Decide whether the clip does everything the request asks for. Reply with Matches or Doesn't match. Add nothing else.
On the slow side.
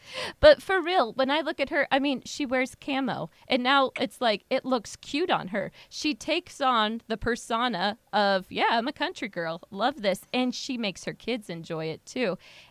Doesn't match